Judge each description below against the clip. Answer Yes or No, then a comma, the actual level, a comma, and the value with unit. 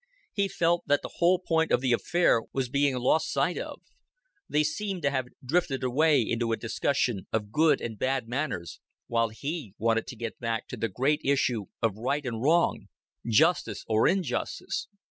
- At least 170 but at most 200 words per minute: Yes, average, 180 wpm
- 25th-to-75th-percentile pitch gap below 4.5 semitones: No, wide, 5.4 semitones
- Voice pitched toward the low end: Yes, low, 130 Hz